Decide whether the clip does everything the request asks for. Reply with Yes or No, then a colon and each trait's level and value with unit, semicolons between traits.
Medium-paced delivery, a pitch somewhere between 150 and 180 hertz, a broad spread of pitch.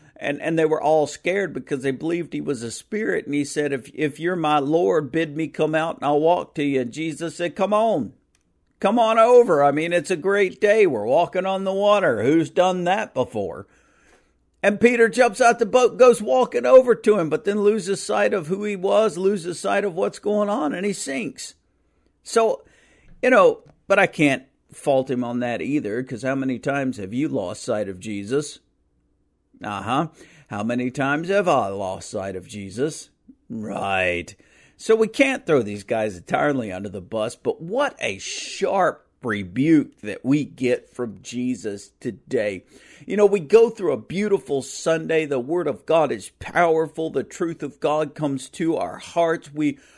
Yes: average, 190 wpm; medium, 160 Hz; wide, 7.3 semitones